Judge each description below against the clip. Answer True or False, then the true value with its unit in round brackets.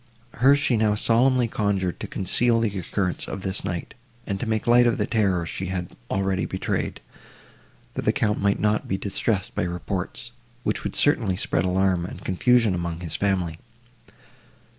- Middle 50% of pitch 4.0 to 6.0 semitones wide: False (3.6 semitones)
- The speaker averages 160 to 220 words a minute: True (170 wpm)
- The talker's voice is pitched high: False (100 Hz)